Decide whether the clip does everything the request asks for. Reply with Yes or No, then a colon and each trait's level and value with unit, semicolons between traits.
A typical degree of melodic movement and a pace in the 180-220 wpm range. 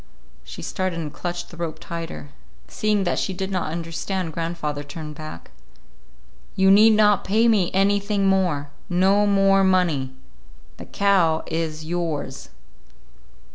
No: average, 3.6 semitones; slow, 135 wpm